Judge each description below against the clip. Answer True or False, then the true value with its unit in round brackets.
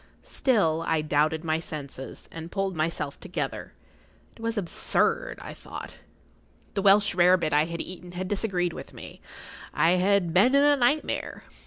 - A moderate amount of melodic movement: True (4.0 semitones)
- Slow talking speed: False (160 wpm)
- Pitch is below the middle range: False (180 Hz)